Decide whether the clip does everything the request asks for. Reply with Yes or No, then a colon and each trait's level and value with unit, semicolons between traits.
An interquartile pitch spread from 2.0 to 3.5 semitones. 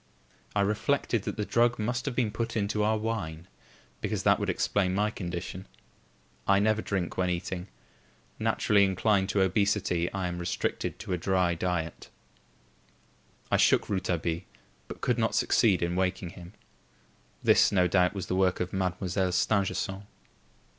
Yes: average, 2.7 semitones